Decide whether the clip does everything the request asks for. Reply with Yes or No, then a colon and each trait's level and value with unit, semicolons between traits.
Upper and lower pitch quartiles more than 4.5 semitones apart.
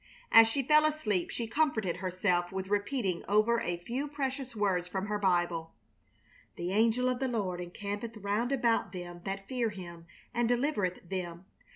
Yes: average, 4.9 semitones